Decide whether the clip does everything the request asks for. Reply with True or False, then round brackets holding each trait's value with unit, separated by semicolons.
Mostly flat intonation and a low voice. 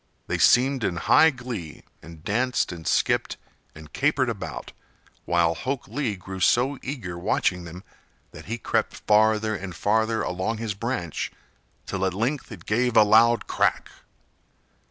False (5.2 semitones; 110 Hz)